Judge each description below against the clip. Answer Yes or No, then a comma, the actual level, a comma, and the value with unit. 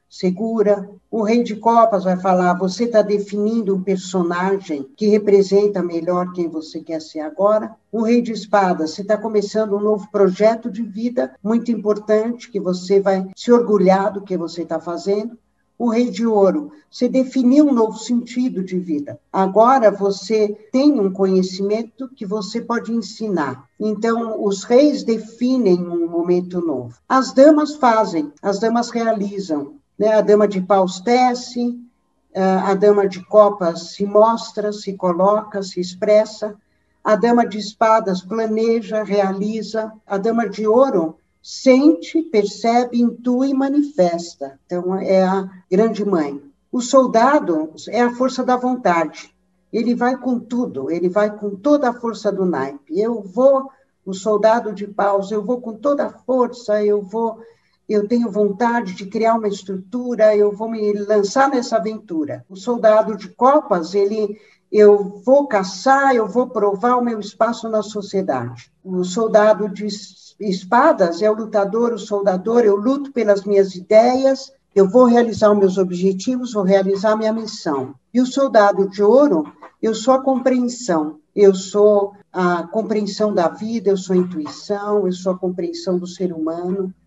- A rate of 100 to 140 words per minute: No, average, 155 wpm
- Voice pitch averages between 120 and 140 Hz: No, high, 210 Hz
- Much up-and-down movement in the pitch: No, average, 3.4 semitones